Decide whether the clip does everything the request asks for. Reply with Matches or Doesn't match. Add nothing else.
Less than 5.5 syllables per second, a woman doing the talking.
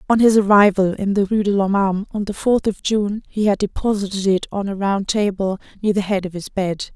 Doesn't match